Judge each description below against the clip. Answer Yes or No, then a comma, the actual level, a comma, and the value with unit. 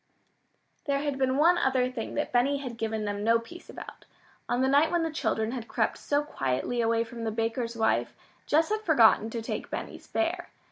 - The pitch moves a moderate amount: Yes, average, 4.6 semitones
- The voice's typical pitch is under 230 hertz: No, very high, 250 Hz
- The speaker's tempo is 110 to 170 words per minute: No, average, 200 wpm